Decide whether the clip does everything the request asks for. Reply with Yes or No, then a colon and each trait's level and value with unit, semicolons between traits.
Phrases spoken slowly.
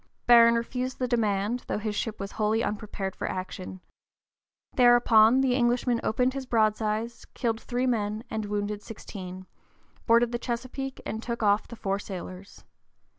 No: average, 150 wpm